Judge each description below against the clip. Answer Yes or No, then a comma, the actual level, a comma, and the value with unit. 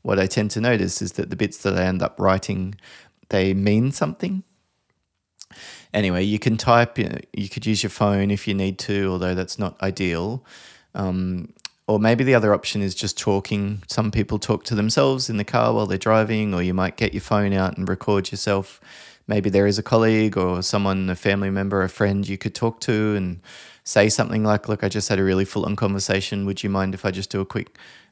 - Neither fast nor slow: No, fast, 220 wpm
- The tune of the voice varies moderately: No, narrow, 2.0 semitones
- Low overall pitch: Yes, low, 100 Hz